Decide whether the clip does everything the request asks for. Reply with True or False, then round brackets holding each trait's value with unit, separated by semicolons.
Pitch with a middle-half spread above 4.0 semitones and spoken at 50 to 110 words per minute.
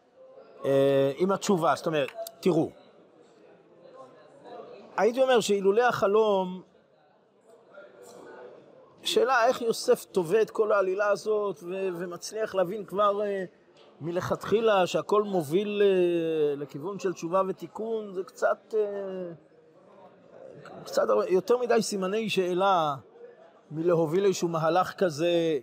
False (3.3 semitones; 100 wpm)